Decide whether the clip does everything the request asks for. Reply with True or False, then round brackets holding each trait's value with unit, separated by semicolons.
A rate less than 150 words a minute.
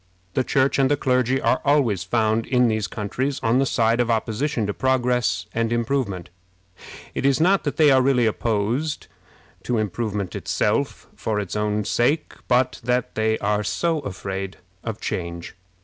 False (165 wpm)